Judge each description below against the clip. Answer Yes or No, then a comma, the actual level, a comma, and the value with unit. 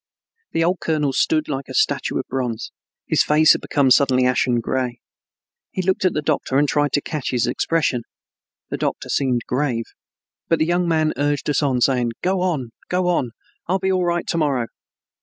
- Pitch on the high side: No, medium, 145 Hz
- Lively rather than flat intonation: No, average, 4.5 semitones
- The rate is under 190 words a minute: No, average, 195 wpm